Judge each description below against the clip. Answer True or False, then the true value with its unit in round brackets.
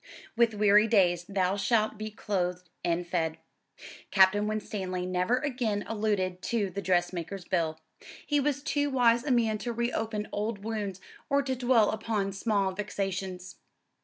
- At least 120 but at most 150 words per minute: True (145 wpm)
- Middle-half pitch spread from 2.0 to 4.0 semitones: True (3.7 semitones)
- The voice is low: False (205 Hz)